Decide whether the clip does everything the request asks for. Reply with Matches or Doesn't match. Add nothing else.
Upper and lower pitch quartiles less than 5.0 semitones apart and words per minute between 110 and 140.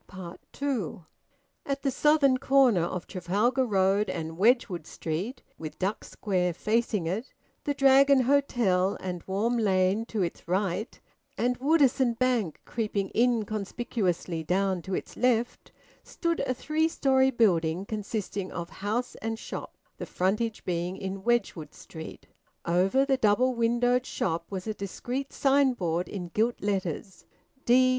Doesn't match